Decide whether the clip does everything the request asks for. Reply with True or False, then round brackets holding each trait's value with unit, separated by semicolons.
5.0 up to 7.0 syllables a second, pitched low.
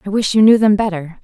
False (6.4 syllables/s; 200 Hz)